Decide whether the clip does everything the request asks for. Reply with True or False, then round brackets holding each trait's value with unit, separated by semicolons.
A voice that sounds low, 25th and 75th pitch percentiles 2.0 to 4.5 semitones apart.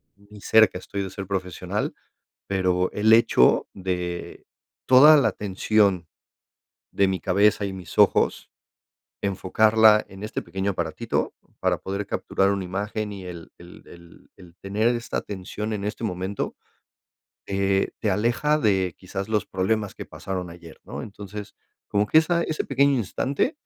True (100 Hz; 2.5 semitones)